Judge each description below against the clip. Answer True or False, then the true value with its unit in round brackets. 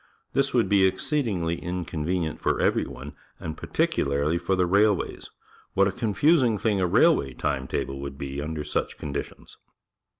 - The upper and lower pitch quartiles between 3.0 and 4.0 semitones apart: False (5.6 semitones)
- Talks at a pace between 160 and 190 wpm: True (170 wpm)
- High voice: False (90 Hz)